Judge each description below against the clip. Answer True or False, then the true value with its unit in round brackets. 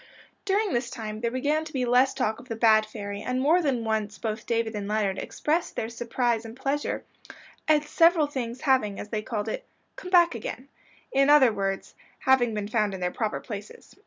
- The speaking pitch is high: True (235 Hz)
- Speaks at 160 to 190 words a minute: False (200 wpm)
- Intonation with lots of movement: False (4.2 semitones)